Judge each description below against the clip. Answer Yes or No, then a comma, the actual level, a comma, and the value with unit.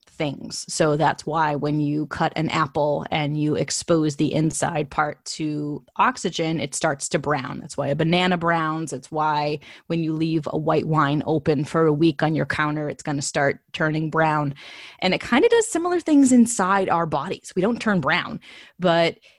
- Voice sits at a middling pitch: Yes, medium, 155 Hz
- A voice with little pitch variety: Yes, narrow, 2.2 semitones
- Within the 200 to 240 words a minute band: No, average, 190 wpm